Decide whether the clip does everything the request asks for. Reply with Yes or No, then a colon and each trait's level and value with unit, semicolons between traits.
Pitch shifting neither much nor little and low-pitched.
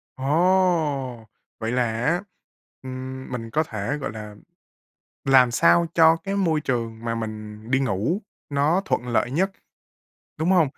No: wide, 5.9 semitones; low, 130 Hz